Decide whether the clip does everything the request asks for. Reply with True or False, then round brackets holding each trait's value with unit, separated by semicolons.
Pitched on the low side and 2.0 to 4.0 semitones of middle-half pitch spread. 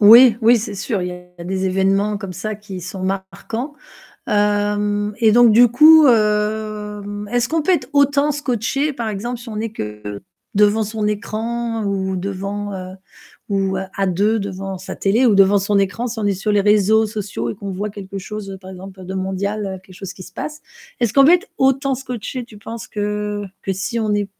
False (210 Hz; 2.9 semitones)